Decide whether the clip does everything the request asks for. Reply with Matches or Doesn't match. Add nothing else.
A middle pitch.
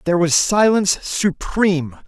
Matches